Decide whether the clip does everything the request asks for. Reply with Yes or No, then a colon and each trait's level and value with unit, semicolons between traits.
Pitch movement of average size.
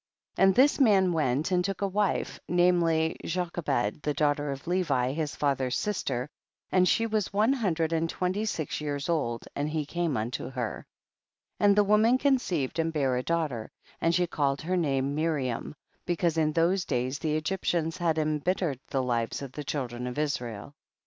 Yes: average, 4.7 semitones